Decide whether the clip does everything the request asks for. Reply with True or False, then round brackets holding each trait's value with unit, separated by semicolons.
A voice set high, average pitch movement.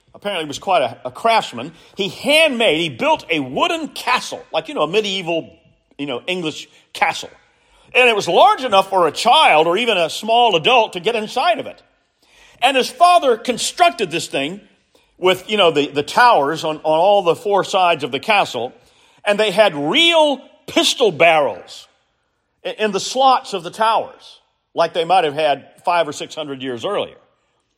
False (205 Hz; 7.5 semitones)